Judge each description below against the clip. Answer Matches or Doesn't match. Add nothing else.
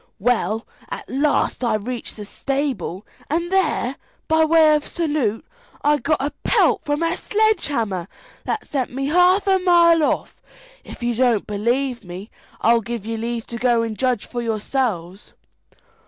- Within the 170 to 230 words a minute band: Doesn't match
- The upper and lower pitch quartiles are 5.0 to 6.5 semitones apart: Matches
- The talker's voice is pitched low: Doesn't match